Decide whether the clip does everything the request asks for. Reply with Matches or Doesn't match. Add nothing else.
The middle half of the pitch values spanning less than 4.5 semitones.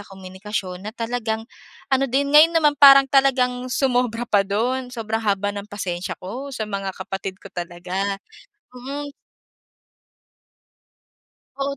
Doesn't match